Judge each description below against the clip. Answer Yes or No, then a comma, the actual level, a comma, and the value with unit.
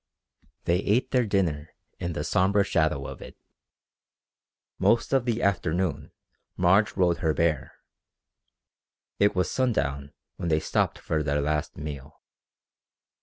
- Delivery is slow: Yes, slow, 125 wpm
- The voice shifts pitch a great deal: No, average, 4.8 semitones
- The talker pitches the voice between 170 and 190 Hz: No, very low, 85 Hz